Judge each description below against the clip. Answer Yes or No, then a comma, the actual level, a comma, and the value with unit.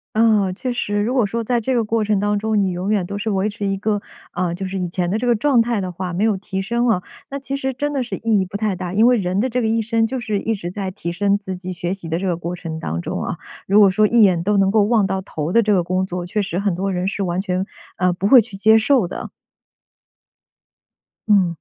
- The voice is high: Yes, high, 200 Hz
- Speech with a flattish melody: No, average, 3.3 semitones